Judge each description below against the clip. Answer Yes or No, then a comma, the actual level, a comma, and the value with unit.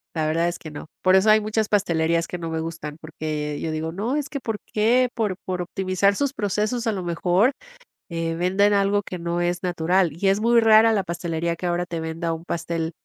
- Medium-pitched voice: Yes, medium, 180 Hz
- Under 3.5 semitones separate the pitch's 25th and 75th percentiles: No, average, 4.0 semitones